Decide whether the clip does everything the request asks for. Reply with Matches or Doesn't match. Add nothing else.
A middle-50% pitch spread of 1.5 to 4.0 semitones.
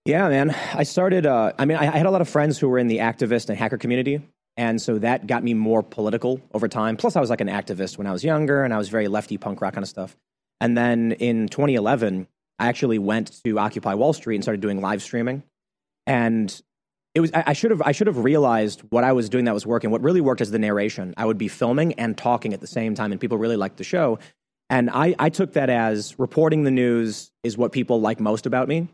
Doesn't match